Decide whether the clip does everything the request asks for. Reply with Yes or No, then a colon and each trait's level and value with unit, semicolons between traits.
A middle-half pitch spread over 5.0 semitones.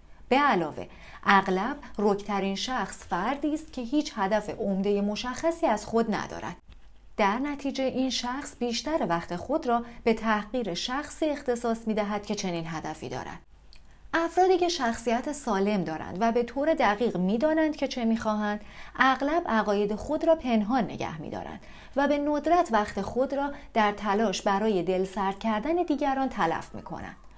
Yes: wide, 5.5 semitones